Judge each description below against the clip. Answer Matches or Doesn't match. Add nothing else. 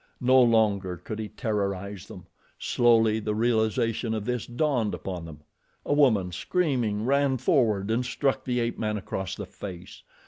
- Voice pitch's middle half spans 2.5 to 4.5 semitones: Matches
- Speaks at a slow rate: Doesn't match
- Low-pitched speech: Matches